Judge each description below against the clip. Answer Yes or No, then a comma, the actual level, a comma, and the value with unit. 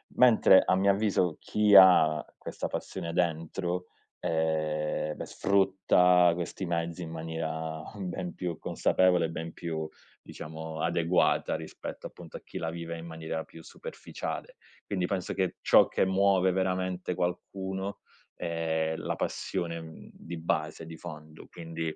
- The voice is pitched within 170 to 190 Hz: No, very low, 85 Hz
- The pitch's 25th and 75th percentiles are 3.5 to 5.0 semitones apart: No, narrow, 2.5 semitones